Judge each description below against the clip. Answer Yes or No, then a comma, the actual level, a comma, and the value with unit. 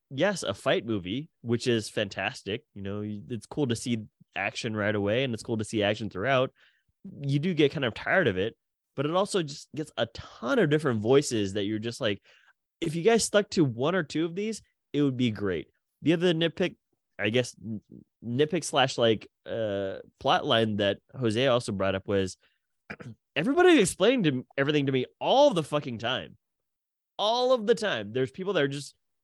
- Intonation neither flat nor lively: No, wide, 6.6 semitones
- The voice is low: Yes, low, 130 Hz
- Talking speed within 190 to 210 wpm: Yes, average, 195 wpm